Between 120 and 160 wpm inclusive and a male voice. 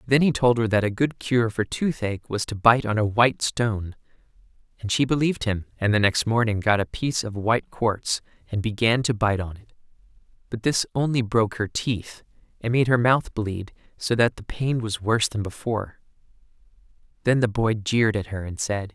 No: fast, 205 wpm; male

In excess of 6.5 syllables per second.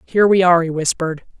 Yes: 7.8 syllables/s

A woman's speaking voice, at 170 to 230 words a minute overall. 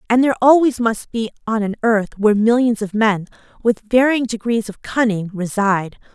Yes: female; average, 175 wpm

